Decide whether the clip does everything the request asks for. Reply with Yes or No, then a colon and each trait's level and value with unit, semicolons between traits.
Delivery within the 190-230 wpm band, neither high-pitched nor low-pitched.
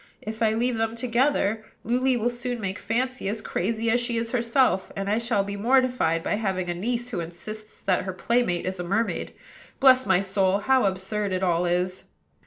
No: average, 195 wpm; high, 220 Hz